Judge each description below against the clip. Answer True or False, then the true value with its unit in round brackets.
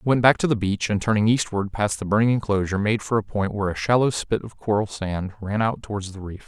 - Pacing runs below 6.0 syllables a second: False (6.2 syllables/s)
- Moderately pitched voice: False (105 Hz)